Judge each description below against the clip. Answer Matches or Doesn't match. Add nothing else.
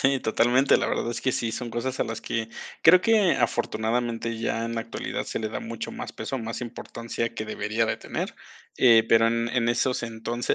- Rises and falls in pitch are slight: Matches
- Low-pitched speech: Matches